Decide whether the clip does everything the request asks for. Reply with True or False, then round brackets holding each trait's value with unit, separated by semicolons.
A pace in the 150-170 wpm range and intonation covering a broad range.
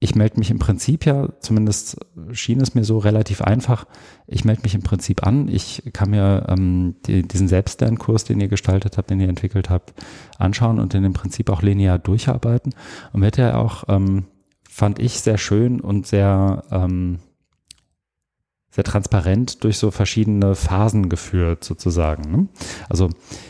False (165 wpm; 3.0 semitones)